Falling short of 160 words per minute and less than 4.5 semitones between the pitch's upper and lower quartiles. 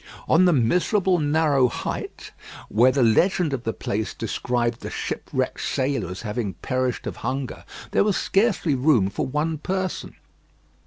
No: average, 150 wpm; wide, 5.6 semitones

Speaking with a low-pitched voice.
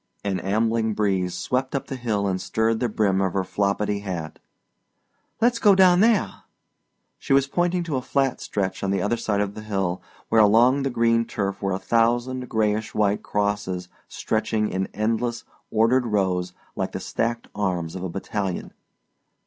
Yes: low, 105 Hz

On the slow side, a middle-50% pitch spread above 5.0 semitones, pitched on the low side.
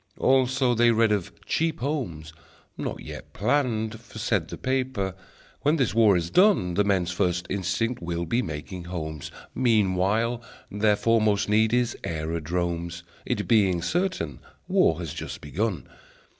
No: average, 145 wpm; wide, 5.5 semitones; low, 105 Hz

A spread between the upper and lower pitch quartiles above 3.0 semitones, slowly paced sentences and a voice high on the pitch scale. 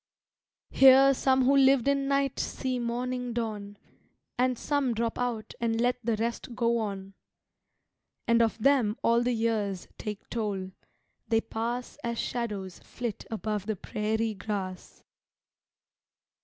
No: average, 2.7 semitones; slow, 130 wpm; high, 235 Hz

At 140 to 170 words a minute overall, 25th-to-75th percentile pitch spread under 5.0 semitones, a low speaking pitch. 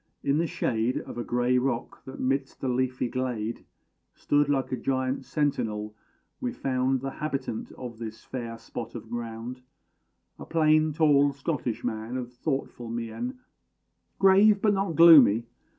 Yes: average, 150 wpm; average, 3.6 semitones; low, 130 Hz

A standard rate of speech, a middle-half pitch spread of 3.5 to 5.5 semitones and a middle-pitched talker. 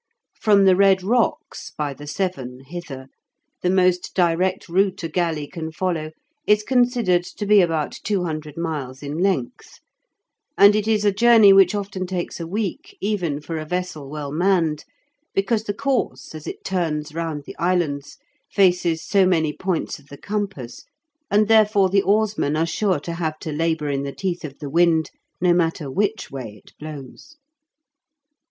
Yes: average, 165 wpm; average, 4.4 semitones; medium, 175 Hz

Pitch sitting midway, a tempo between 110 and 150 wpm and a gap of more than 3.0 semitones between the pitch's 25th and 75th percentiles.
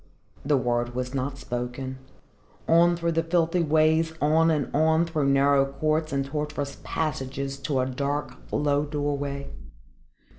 No: medium, 145 Hz; average, 140 wpm; narrow, 2.6 semitones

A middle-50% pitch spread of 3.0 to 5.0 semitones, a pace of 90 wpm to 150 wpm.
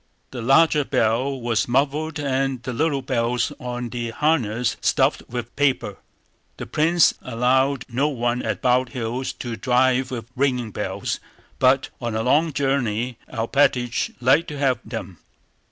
No: narrow, 2.6 semitones; average, 145 wpm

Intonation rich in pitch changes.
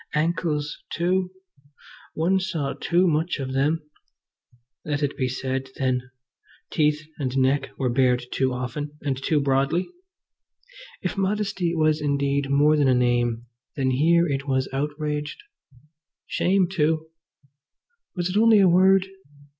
No: average, 4.2 semitones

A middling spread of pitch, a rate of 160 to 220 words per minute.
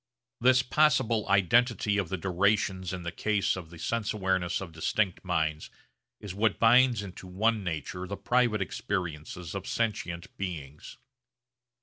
No: average, 3.7 semitones; average, 140 wpm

